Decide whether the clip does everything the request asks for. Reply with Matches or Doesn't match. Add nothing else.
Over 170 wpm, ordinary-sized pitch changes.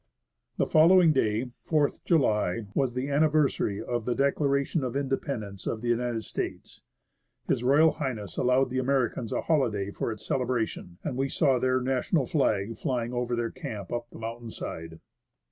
Doesn't match